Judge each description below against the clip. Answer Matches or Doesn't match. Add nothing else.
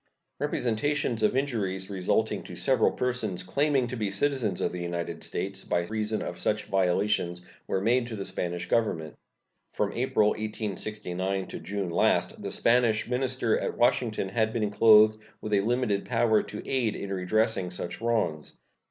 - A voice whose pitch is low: Matches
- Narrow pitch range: Doesn't match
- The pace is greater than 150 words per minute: Matches